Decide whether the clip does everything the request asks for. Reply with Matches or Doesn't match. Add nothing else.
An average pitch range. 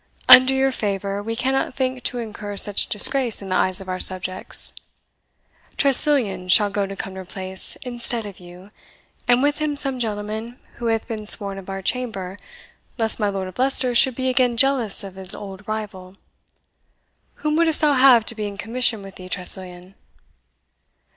Matches